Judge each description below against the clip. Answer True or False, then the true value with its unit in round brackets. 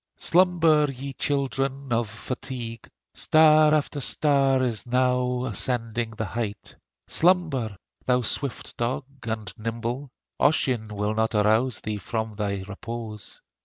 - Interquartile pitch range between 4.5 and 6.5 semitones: False (3.8 semitones)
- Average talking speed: False (120 wpm)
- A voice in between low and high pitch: False (125 Hz)